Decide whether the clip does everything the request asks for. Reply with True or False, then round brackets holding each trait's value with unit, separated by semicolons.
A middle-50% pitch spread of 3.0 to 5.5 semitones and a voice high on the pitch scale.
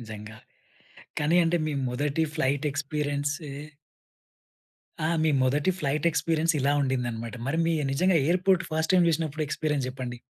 False (3.4 semitones; 150 Hz)